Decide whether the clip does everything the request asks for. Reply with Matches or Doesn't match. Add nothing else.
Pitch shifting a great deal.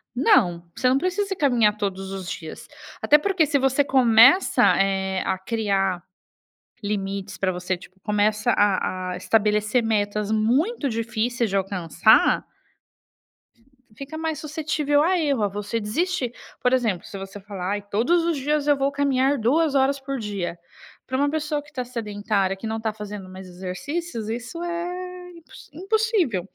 Matches